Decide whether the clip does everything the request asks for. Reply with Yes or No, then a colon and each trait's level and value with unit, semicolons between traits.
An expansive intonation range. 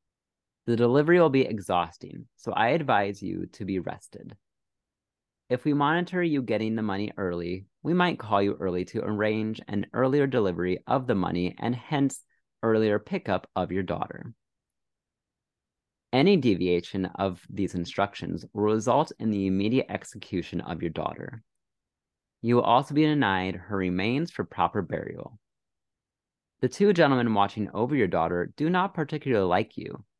Yes: wide, 5.9 semitones